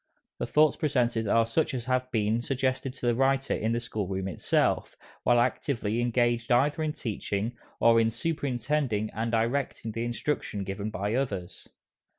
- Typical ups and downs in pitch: Yes, average, 3.1 semitones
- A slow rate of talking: No, average, 165 wpm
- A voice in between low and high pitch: No, low, 120 Hz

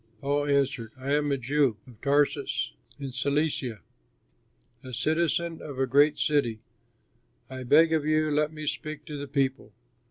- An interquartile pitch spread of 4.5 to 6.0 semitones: No, narrow, 2.5 semitones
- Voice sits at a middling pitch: Yes, medium, 145 Hz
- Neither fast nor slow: Yes, average, 155 wpm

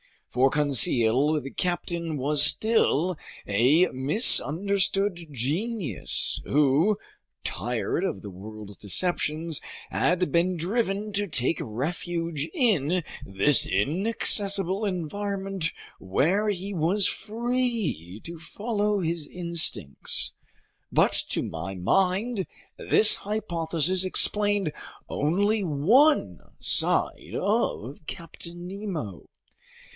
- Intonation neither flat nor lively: No, wide, 5.9 semitones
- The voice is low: No, medium, 170 Hz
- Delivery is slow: Yes, slow, 90 wpm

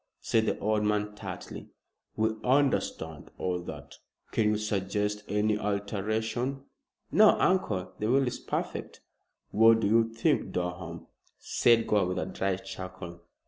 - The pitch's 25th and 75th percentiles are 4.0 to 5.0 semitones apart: No, average, 2.7 semitones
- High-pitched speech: No, low, 105 Hz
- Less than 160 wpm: Yes, average, 140 wpm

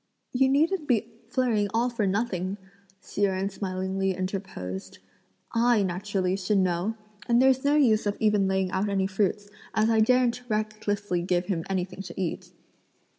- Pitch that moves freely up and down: No, average, 3.4 semitones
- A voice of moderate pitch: No, high, 205 Hz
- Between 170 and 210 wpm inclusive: No, average, 155 wpm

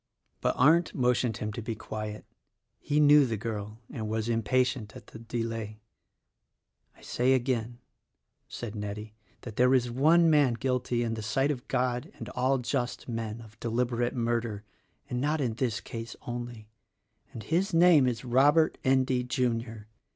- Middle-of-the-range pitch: No, low, 120 Hz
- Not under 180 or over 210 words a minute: No, average, 160 wpm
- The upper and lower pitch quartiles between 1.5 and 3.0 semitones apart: Yes, narrow, 2.6 semitones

